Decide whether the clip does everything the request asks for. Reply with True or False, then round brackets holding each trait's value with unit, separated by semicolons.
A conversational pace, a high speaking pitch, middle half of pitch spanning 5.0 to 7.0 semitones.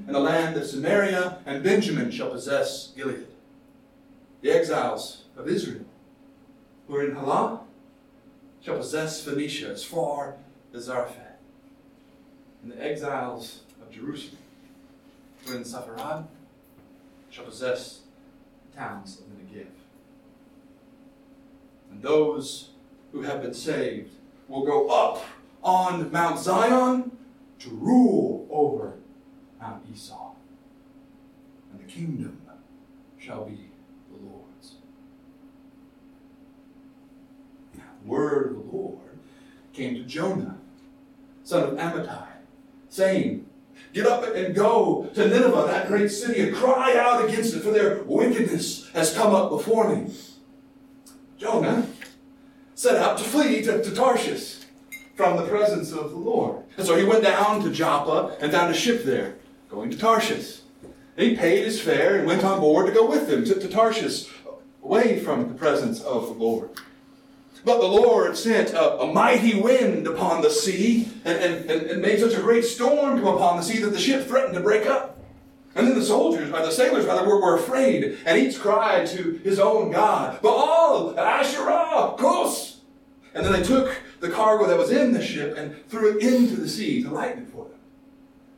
True (150 wpm; 250 Hz; 5.6 semitones)